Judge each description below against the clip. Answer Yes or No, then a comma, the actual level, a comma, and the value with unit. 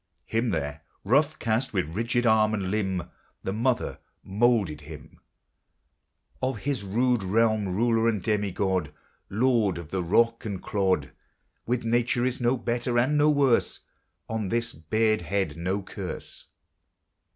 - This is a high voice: No, low, 110 Hz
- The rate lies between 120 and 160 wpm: Yes, average, 140 wpm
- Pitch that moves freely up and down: No, average, 4.0 semitones